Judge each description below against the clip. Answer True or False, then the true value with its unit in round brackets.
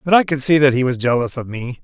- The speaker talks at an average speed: False (325 wpm)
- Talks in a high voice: False (135 Hz)